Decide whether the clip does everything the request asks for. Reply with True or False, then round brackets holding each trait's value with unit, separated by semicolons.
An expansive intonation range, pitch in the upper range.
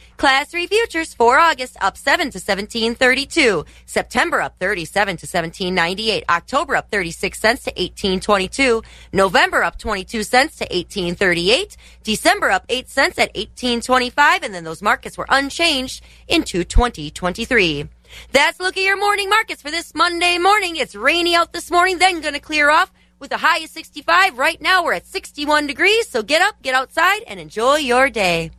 True (8.9 semitones; 260 Hz)